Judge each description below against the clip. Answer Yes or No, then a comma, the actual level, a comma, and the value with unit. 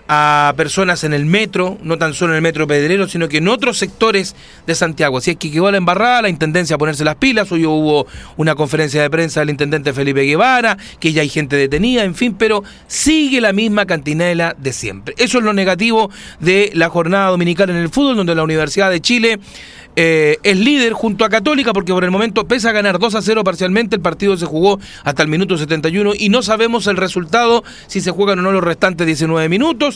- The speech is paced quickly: Yes, fast, 220 wpm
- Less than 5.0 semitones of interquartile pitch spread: No, wide, 5.5 semitones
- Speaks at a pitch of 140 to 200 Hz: Yes, medium, 185 Hz